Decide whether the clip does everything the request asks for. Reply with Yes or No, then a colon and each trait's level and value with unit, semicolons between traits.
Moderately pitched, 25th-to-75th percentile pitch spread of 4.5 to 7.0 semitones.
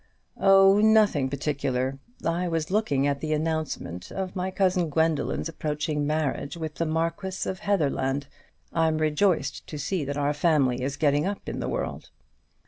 No: medium, 155 Hz; average, 4.1 semitones